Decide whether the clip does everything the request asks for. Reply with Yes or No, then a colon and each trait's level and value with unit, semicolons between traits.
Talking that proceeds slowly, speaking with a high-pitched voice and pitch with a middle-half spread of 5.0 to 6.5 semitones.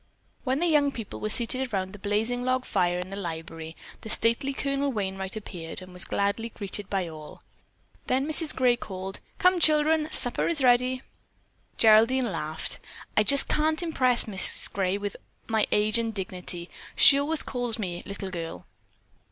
No: average, 165 wpm; high, 220 Hz; wide, 5.5 semitones